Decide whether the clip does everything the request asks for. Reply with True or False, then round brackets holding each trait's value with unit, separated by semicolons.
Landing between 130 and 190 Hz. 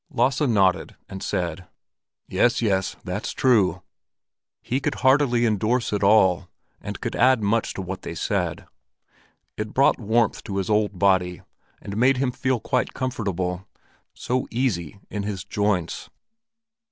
False (105 Hz)